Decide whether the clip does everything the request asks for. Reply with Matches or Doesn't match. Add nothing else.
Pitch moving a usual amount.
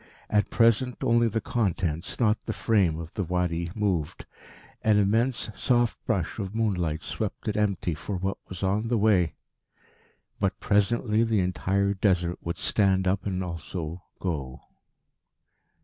Matches